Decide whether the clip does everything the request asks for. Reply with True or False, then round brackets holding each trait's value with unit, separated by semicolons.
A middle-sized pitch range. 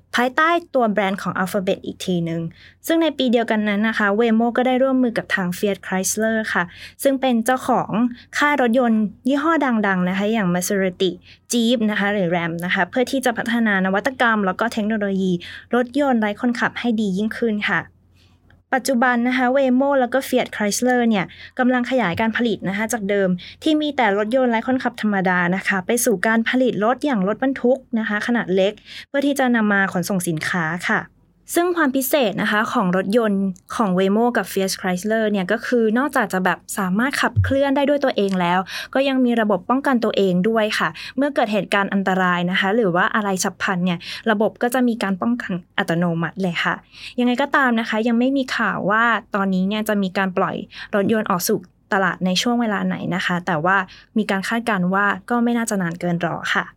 True (4.5 semitones)